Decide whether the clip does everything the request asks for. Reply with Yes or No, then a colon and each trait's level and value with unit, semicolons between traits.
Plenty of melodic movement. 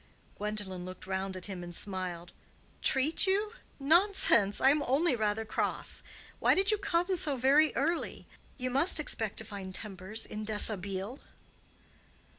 Yes: wide, 7.9 semitones